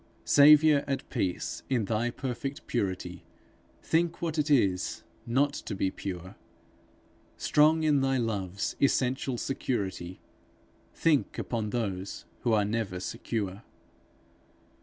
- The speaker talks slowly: Yes, slow, 115 wpm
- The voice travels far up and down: Yes, wide, 6.4 semitones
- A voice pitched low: Yes, low, 120 Hz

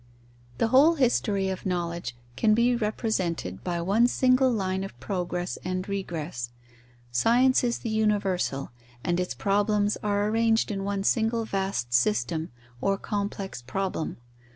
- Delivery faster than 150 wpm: No, slow, 135 wpm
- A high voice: Yes, high, 195 Hz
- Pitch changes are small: No, average, 4.2 semitones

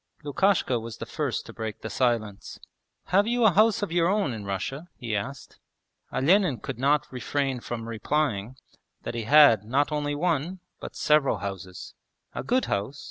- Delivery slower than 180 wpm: Yes, average, 170 wpm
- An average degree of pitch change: No, wide, 6.7 semitones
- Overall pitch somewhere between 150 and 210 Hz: No, medium, 140 Hz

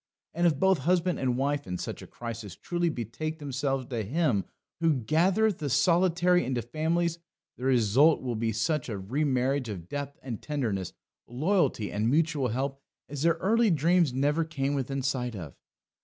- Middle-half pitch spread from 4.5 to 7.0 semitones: Yes, average, 5.2 semitones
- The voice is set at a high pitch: No, medium, 140 Hz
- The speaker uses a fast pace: No, average, 170 wpm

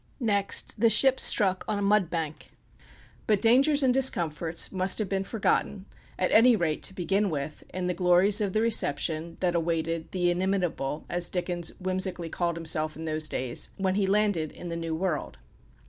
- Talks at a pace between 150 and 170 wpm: No, average, 180 wpm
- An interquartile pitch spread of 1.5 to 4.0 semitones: Yes, average, 3.5 semitones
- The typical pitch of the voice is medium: Yes, medium, 180 Hz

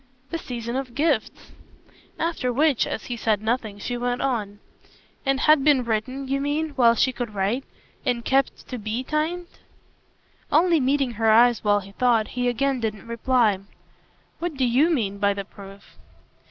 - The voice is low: No, high, 245 Hz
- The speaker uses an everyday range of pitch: Yes, average, 3.9 semitones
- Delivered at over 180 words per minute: No, average, 170 wpm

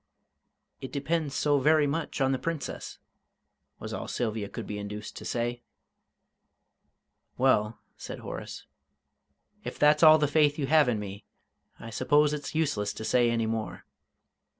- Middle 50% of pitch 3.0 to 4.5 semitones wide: No, average, 4.9 semitones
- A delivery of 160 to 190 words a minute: No, average, 150 wpm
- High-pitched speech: No, low, 135 Hz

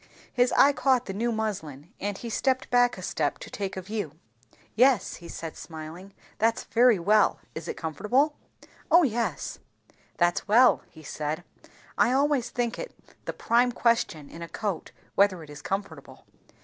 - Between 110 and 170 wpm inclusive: Yes, average, 165 wpm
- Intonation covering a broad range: Yes, wide, 6.4 semitones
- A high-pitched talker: Yes, high, 210 Hz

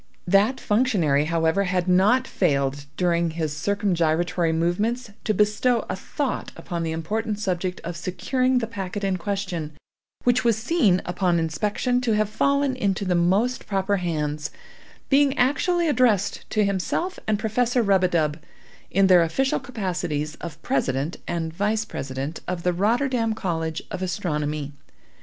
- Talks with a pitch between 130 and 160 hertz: No, high, 190 Hz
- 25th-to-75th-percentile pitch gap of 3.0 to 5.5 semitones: Yes, average, 5.1 semitones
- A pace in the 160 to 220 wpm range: No, average, 145 wpm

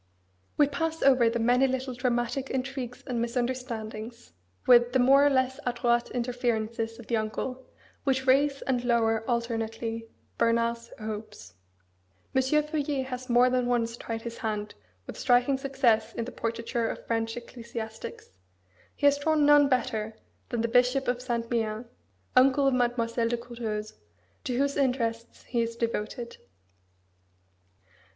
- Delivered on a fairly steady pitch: Yes, narrow, 2.2 semitones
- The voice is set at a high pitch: Yes, high, 240 Hz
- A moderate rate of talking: Yes, average, 145 wpm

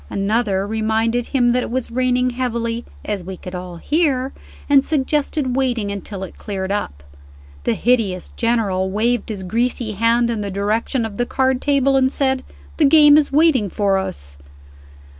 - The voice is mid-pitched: No, high, 235 Hz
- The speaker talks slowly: No, average, 165 wpm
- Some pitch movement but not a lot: Yes, average, 4.5 semitones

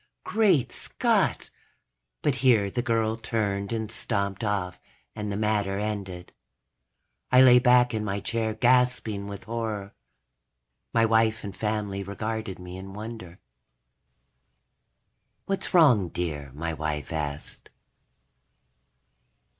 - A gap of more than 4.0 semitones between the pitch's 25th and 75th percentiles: No, average, 2.9 semitones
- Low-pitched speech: Yes, low, 105 Hz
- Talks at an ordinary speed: No, slow, 115 wpm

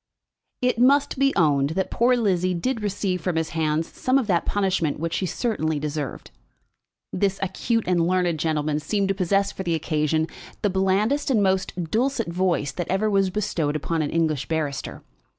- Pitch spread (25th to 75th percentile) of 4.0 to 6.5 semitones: Yes, average, 4.3 semitones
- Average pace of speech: Yes, average, 175 wpm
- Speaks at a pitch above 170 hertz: Yes, medium, 185 Hz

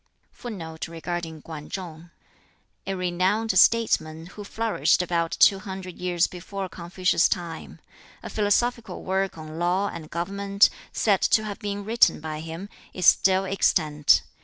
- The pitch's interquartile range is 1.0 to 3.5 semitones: Yes, average, 3.2 semitones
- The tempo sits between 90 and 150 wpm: Yes, slow, 135 wpm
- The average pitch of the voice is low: No, medium, 185 Hz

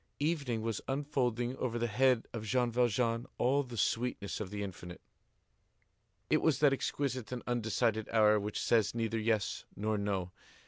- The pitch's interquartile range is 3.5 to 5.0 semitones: No, average, 3.0 semitones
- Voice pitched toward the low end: Yes, low, 115 Hz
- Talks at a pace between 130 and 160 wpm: Yes, average, 155 wpm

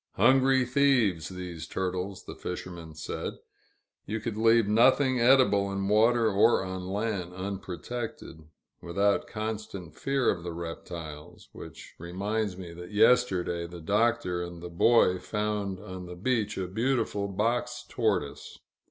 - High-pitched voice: No, low, 100 Hz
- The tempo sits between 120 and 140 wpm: Yes, slow, 135 wpm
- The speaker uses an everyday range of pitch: Yes, average, 4.4 semitones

